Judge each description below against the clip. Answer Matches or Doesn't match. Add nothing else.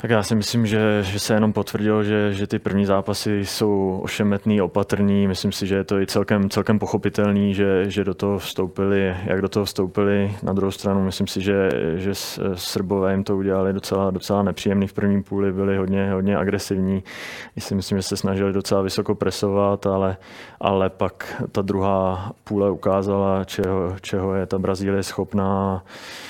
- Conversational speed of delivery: Doesn't match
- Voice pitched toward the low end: Matches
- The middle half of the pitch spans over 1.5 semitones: Doesn't match